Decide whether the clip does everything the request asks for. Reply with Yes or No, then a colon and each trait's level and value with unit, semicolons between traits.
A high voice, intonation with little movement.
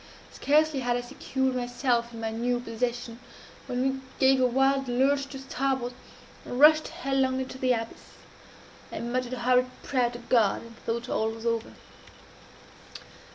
Yes: very high, 250 Hz; narrow, 2.0 semitones